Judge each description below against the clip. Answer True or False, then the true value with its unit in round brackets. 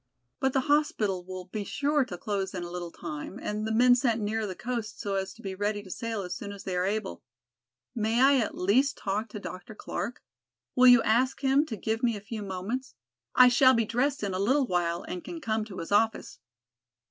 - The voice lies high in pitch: True (220 Hz)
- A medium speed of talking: False (225 wpm)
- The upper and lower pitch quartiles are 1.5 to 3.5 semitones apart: False (4.4 semitones)